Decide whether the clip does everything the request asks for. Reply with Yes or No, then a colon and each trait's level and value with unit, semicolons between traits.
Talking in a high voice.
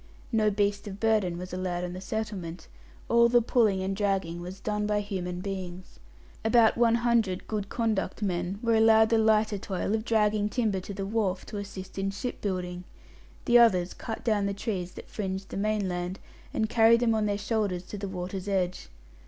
Yes: high, 200 Hz